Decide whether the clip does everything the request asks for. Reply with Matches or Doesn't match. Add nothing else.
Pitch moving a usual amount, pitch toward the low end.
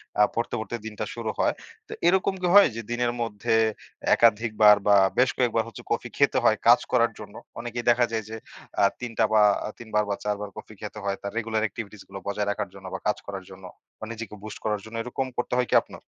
Doesn't match